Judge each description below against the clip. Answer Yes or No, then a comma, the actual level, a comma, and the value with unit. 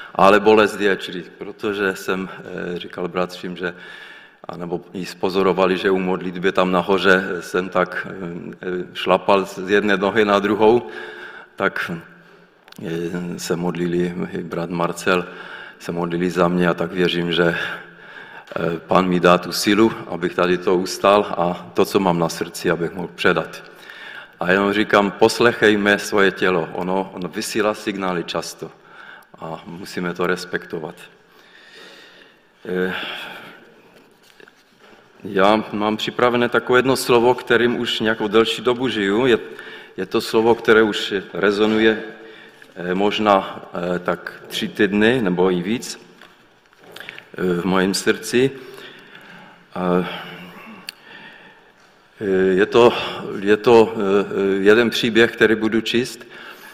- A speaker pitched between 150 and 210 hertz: No, very low, 95 Hz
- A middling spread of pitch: Yes, average, 3.4 semitones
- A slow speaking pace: Yes, slow, 110 wpm